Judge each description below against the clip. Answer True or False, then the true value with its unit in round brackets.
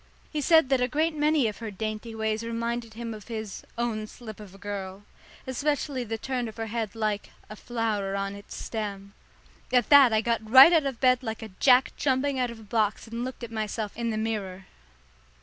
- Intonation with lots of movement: False (2.9 semitones)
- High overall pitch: True (225 Hz)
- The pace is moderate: False (210 wpm)